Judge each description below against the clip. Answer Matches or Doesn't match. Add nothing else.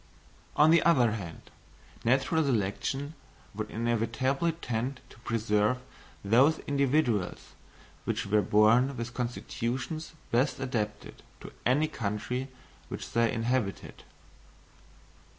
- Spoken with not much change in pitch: Doesn't match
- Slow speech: Matches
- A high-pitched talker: Doesn't match